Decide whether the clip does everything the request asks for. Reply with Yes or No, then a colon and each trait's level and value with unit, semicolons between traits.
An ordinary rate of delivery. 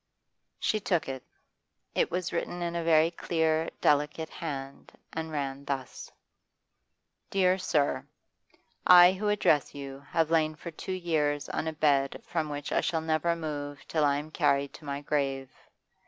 Yes: average, 155 wpm